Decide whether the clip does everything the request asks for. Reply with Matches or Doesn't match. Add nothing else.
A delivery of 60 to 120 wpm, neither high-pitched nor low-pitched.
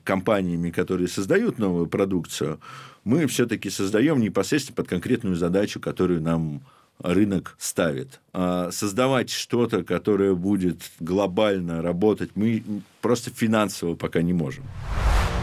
Doesn't match